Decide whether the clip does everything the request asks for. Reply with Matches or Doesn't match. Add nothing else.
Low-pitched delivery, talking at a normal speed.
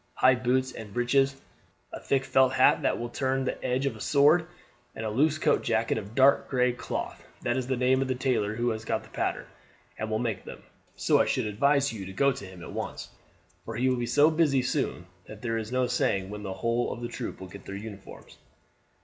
Doesn't match